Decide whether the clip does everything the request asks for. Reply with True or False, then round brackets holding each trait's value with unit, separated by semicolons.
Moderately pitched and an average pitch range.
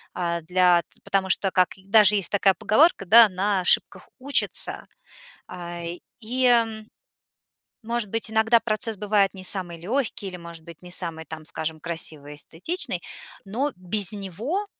False (195 Hz; 4.2 semitones)